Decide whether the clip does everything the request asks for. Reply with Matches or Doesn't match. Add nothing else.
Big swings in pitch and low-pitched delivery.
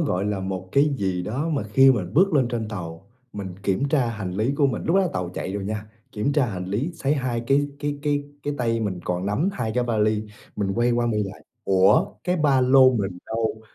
Matches